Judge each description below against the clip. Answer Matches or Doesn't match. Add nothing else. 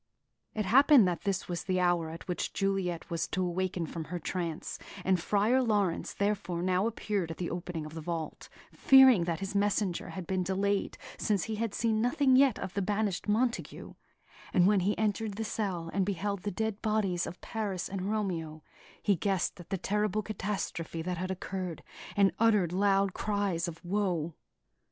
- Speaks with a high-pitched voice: Matches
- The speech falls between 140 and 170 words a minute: Doesn't match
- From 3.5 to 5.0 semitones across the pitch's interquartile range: Doesn't match